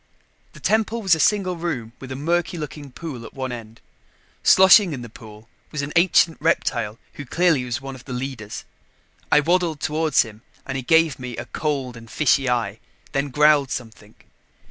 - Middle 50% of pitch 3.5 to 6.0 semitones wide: Yes, average, 5.0 semitones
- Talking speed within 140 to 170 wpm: No, average, 185 wpm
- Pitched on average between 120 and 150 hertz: Yes, medium, 140 Hz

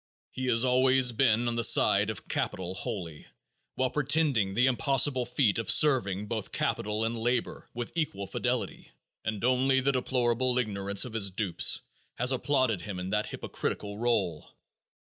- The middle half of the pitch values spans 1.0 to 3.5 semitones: No, average, 4.0 semitones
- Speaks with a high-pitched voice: No, low, 120 Hz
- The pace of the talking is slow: No, average, 155 wpm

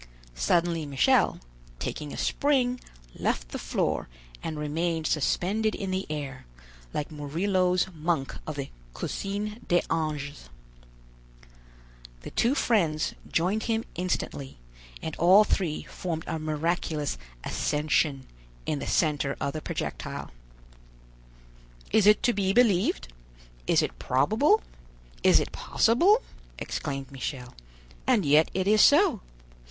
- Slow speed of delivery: Yes, slow, 120 wpm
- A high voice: No, medium, 165 Hz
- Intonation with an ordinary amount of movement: No, wide, 5.8 semitones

